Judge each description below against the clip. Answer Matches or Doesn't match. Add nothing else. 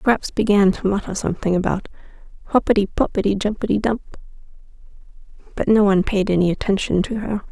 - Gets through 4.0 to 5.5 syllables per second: Doesn't match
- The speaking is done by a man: Doesn't match